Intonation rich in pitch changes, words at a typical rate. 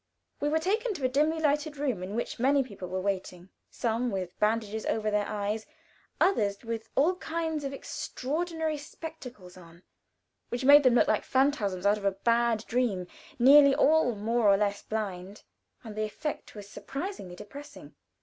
Yes: wide, 6.1 semitones; average, 170 wpm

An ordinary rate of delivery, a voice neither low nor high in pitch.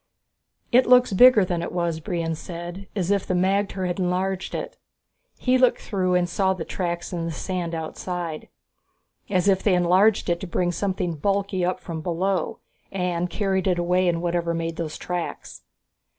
Yes: average, 180 wpm; medium, 180 Hz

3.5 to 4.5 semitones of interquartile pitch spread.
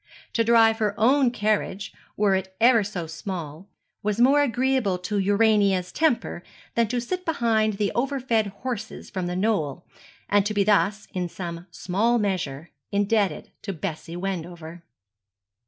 Yes: average, 4.0 semitones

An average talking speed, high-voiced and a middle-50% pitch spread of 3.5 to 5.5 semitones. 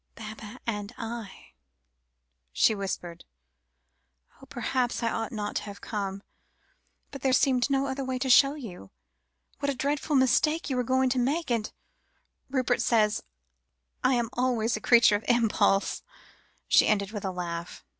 Yes: average, 155 wpm; high, 235 Hz; average, 3.9 semitones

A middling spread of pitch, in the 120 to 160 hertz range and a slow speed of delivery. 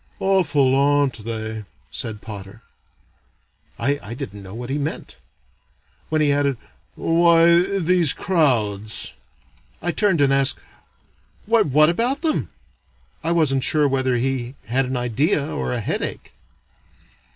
No: wide, 5.7 semitones; medium, 140 Hz; slow, 125 wpm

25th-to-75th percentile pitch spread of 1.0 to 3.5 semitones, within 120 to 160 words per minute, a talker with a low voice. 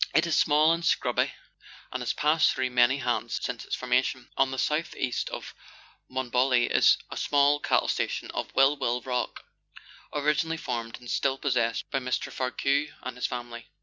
No: average, 2.9 semitones; average, 175 wpm; low, 130 Hz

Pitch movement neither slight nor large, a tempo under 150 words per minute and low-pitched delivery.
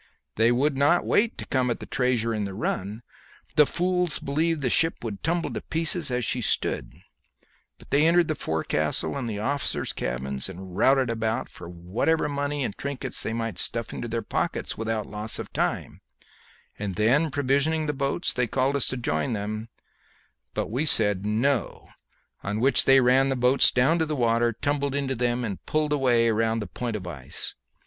No: average, 4.6 semitones; average, 185 wpm; low, 125 Hz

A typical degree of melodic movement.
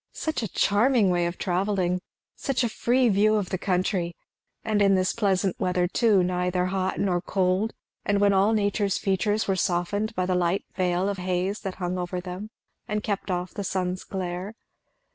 No: narrow, 2.2 semitones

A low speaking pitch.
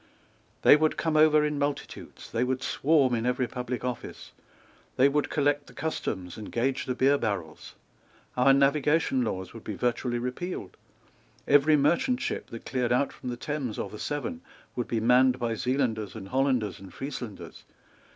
Yes: low, 130 Hz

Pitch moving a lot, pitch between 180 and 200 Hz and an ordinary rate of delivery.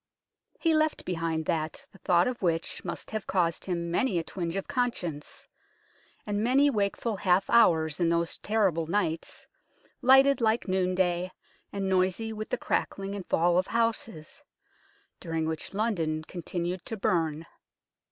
No: average, 4.5 semitones; medium, 185 Hz; average, 150 wpm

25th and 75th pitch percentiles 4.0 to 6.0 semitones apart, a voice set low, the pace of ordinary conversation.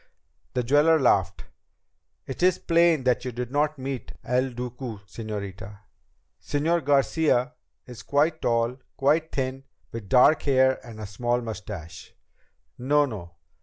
No: average, 4.4 semitones; low, 125 Hz; slow, 130 wpm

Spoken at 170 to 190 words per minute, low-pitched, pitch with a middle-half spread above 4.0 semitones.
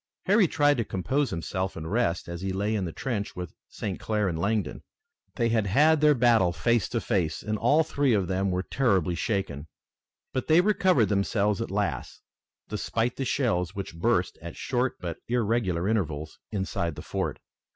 Yes: average, 180 wpm; low, 105 Hz; average, 5.2 semitones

